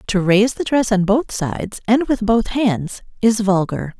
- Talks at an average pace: Yes, average, 195 wpm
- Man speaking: No, female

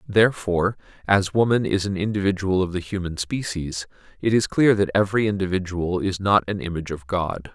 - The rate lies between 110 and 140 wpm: No, average, 175 wpm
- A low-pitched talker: Yes, very low, 95 Hz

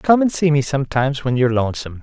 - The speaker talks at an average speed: No, fast, 240 wpm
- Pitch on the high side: No, medium, 140 Hz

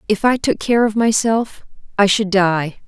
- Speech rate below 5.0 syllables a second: Yes, 4.3 syllables/s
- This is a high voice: Yes, high, 210 Hz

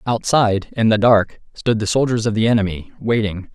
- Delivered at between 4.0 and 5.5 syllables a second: Yes, 5.4 syllables/s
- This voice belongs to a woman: No, male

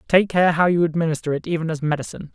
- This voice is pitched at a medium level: Yes, medium, 165 Hz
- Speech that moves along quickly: Yes, fast, 230 wpm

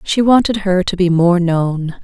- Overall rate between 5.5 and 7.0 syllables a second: No, 4.2 syllables/s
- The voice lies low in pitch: No, medium, 185 Hz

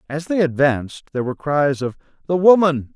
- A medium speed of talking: Yes, average, 185 wpm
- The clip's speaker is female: No, male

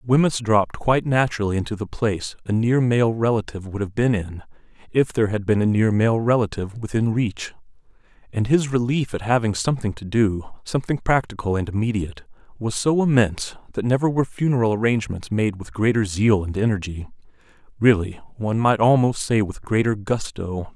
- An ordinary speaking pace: Yes, average, 170 wpm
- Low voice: Yes, low, 110 Hz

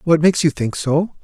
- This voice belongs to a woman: No, male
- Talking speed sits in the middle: No, fast, 240 wpm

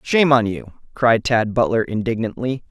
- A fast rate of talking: No, average, 155 wpm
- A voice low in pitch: Yes, low, 115 Hz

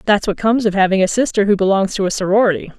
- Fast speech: Yes, fast, 260 wpm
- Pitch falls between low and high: No, high, 200 Hz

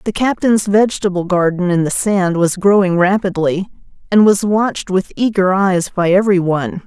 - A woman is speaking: Yes, female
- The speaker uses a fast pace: No, average, 155 wpm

